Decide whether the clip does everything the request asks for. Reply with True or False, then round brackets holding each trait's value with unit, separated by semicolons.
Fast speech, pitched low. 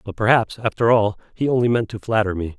True (230 wpm; 110 Hz)